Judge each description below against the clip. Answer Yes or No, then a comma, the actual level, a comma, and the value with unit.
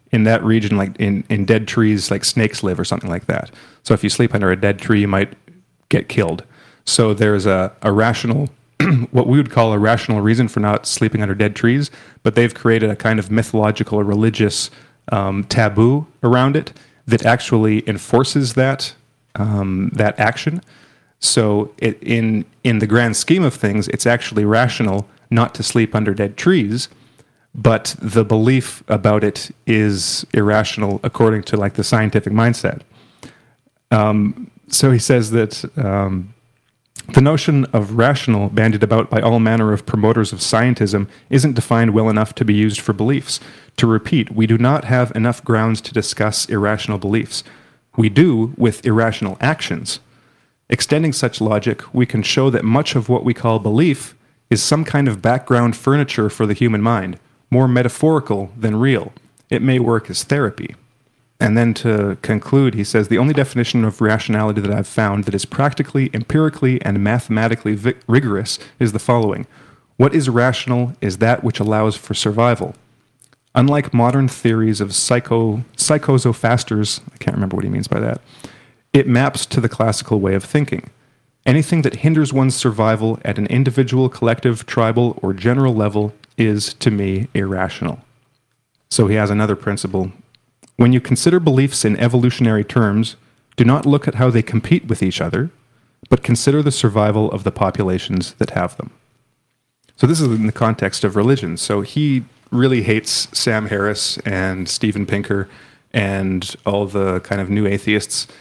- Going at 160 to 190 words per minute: Yes, average, 165 wpm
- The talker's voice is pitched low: Yes, low, 115 Hz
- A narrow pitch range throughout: No, average, 3.3 semitones